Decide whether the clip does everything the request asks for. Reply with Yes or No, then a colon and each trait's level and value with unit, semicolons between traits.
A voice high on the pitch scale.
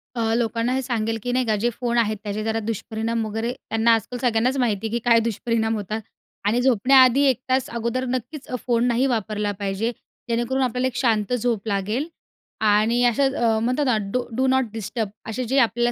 Yes: high, 235 Hz